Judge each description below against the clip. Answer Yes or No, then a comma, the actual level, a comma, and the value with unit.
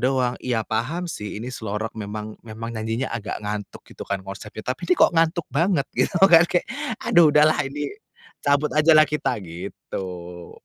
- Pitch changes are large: Yes, wide, 6.6 semitones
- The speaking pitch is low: Yes, low, 120 Hz